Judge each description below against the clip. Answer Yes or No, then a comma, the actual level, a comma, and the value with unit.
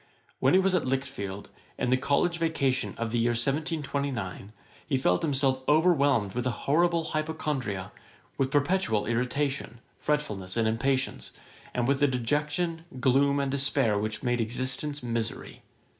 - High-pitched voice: No, low, 135 Hz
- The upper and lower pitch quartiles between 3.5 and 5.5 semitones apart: Yes, average, 4.0 semitones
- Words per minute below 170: Yes, average, 145 wpm